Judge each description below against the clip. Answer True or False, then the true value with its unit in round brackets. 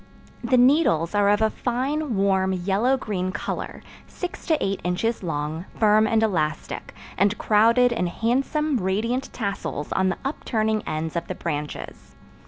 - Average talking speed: True (150 wpm)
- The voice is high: True (210 Hz)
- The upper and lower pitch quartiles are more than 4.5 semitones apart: True (4.9 semitones)